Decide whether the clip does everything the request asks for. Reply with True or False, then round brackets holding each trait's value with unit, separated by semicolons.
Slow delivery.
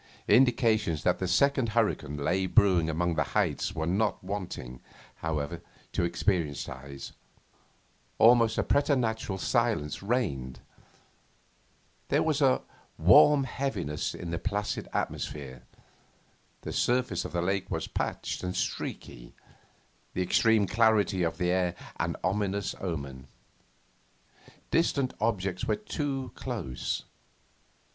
True (115 wpm)